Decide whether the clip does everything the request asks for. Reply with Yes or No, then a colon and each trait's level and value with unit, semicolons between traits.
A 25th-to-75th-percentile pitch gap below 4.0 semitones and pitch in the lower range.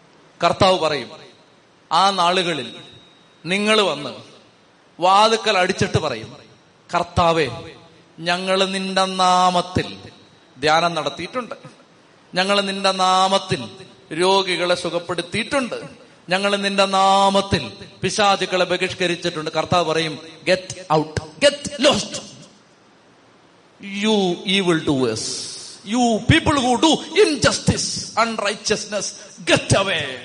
No: average, 2.8 semitones; medium, 185 Hz